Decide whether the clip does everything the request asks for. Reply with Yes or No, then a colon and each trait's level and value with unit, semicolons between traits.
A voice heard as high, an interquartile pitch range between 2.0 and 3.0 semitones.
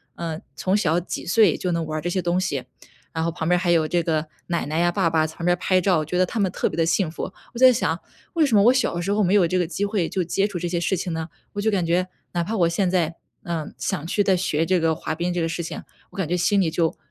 No: medium, 175 Hz; narrow, 2.5 semitones